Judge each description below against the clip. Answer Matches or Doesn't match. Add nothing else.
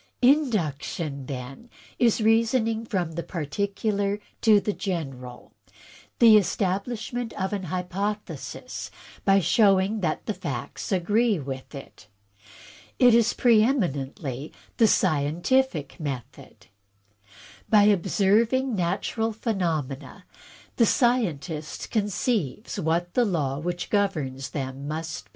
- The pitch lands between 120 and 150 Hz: Doesn't match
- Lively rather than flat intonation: Matches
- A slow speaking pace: Matches